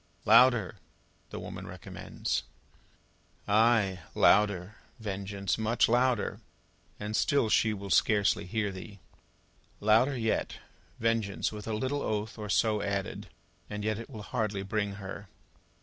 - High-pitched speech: No, low, 105 Hz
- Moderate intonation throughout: No, narrow, 2.0 semitones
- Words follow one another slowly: Yes, slow, 125 wpm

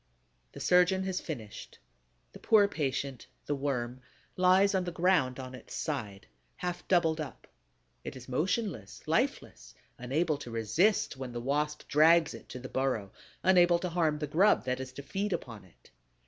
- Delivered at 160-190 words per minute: Yes, average, 165 wpm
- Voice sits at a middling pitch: Yes, medium, 150 Hz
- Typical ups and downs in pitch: No, wide, 5.8 semitones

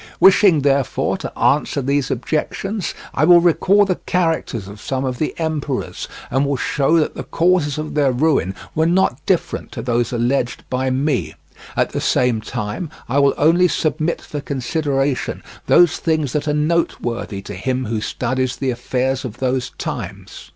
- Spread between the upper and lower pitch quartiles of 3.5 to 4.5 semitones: Yes, average, 3.9 semitones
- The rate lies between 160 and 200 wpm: Yes, average, 165 wpm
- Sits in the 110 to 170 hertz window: Yes, medium, 140 Hz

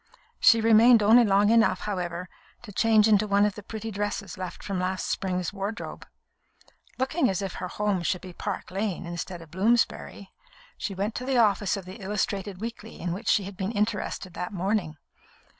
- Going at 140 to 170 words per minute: No, average, 185 wpm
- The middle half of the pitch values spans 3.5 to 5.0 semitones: No, average, 2.8 semitones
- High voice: Yes, high, 200 Hz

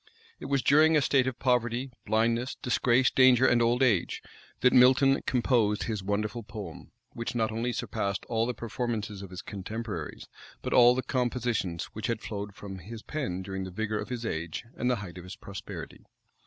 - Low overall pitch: Yes, low, 115 Hz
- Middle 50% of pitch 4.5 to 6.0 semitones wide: No, average, 3.5 semitones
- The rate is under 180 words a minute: No, average, 185 wpm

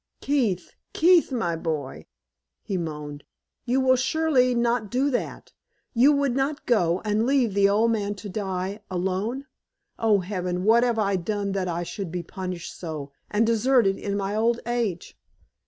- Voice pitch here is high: Yes, high, 210 Hz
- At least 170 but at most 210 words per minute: No, average, 160 wpm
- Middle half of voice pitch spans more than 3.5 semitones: Yes, average, 5.1 semitones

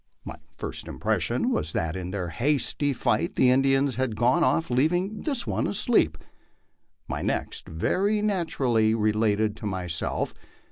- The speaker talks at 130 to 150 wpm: Yes, average, 140 wpm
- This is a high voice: No, low, 125 Hz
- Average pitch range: No, wide, 8.0 semitones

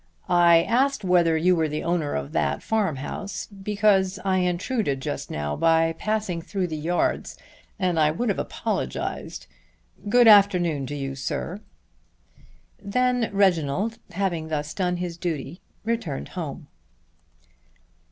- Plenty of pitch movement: No, average, 4.3 semitones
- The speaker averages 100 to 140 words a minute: Yes, slow, 135 wpm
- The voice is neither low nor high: Yes, medium, 175 Hz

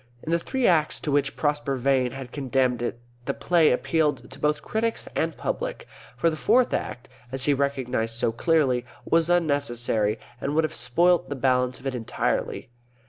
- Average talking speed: Yes, average, 180 wpm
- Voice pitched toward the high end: No, medium, 140 Hz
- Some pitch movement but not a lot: Yes, average, 4.3 semitones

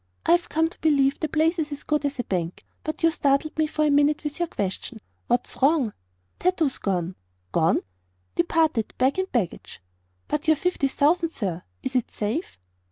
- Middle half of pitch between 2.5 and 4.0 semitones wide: No, average, 4.7 semitones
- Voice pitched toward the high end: Yes, very high, 290 Hz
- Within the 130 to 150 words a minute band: No, average, 180 wpm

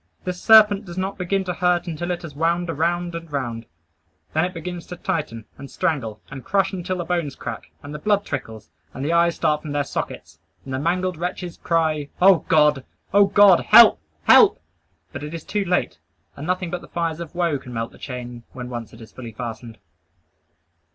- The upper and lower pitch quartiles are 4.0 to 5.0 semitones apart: Yes, average, 4.5 semitones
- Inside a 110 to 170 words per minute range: No, fast, 205 wpm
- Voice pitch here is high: No, medium, 165 Hz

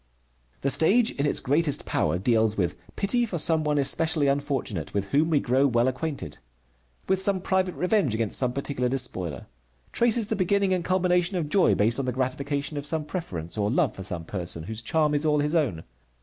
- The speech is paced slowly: No, average, 195 wpm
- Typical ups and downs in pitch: No, wide, 6.7 semitones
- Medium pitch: Yes, medium, 145 Hz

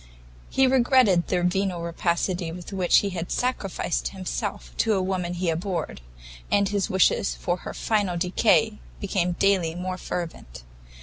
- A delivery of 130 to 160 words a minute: Yes, average, 145 wpm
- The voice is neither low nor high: Yes, medium, 180 Hz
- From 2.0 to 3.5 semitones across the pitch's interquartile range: Yes, narrow, 2.6 semitones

